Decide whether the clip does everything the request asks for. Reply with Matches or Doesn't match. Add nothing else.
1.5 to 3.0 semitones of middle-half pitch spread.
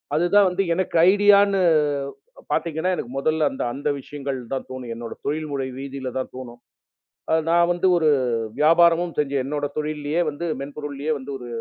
Doesn't match